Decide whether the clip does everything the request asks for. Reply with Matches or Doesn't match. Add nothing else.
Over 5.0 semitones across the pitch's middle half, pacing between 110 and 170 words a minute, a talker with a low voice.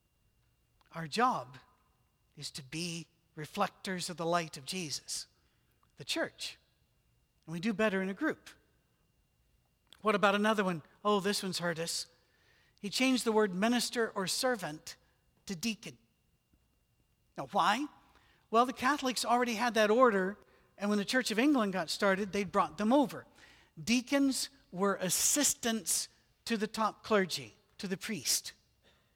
Doesn't match